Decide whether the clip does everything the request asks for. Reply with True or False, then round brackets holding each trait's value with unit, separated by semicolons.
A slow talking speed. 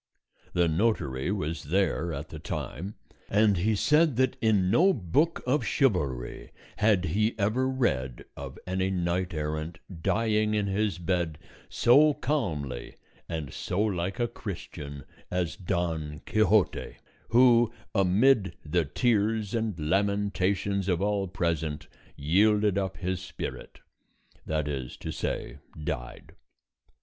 True (125 wpm)